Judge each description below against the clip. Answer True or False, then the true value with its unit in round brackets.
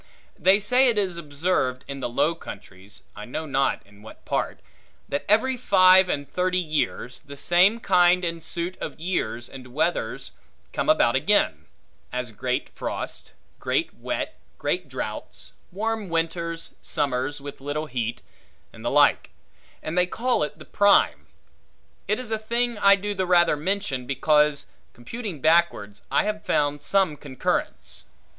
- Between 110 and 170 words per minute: True (150 wpm)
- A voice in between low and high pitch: True (165 Hz)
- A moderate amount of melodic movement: False (6.2 semitones)